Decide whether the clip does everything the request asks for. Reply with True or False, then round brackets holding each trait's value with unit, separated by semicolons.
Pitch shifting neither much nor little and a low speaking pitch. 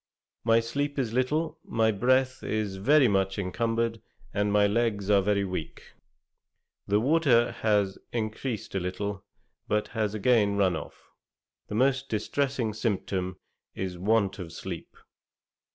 True (3.3 semitones; 110 Hz)